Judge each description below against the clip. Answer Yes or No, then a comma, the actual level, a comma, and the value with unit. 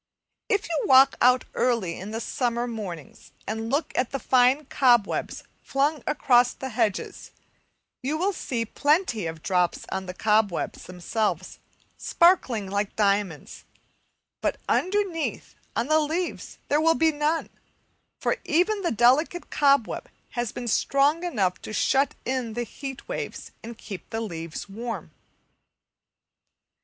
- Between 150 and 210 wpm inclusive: No, slow, 135 wpm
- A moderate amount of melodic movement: No, wide, 6.0 semitones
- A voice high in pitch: Yes, high, 245 Hz